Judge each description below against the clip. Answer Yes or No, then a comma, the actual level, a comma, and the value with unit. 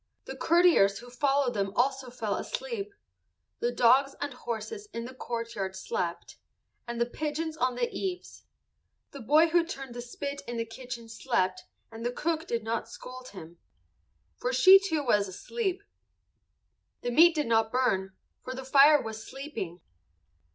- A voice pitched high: Yes, very high, 255 Hz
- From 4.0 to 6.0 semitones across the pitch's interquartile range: Yes, average, 5.2 semitones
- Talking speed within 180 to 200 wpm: No, average, 160 wpm